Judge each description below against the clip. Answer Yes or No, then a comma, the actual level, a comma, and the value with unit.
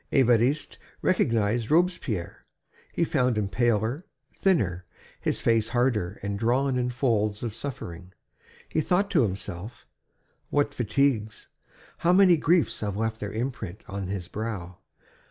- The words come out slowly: Yes, slow, 130 wpm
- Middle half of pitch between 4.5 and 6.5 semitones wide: Yes, average, 5.1 semitones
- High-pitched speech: No, low, 115 Hz